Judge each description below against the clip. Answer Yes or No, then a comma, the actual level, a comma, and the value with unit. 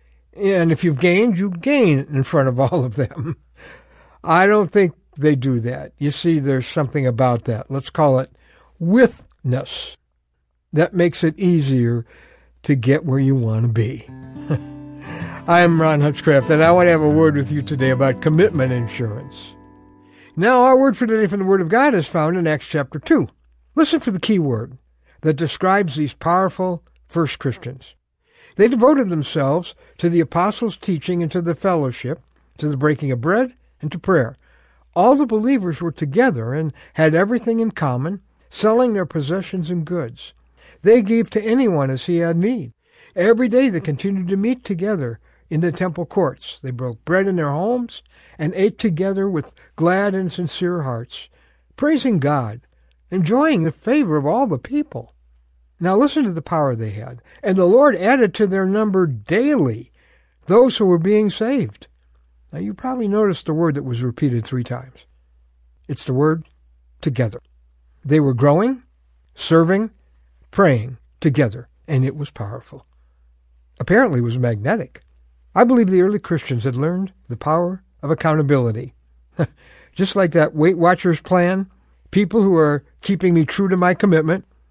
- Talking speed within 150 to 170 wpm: Yes, average, 165 wpm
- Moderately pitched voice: Yes, medium, 155 Hz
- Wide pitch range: Yes, wide, 7.0 semitones